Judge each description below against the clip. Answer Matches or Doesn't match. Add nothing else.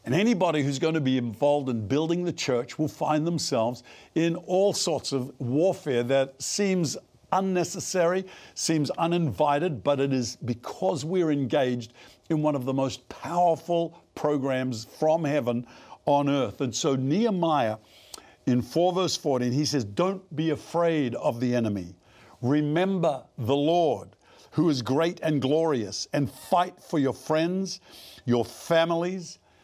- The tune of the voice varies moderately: Matches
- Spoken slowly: Doesn't match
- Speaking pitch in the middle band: Matches